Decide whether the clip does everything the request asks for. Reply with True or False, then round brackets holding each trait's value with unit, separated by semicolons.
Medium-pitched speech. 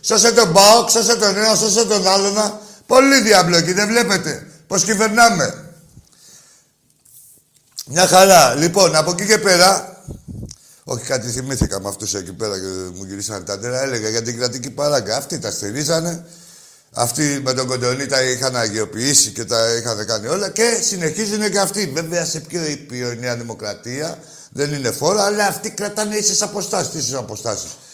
True (160 Hz)